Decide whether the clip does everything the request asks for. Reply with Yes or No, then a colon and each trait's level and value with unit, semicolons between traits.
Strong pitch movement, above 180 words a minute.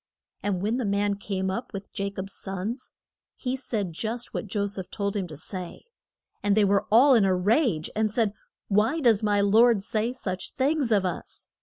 No: average, 3.0 semitones; average, 195 wpm